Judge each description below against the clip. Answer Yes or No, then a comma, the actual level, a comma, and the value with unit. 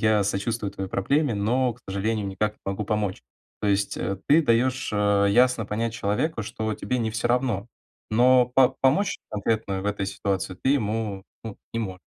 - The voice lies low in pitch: Yes, low, 110 Hz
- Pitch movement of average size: Yes, average, 3.5 semitones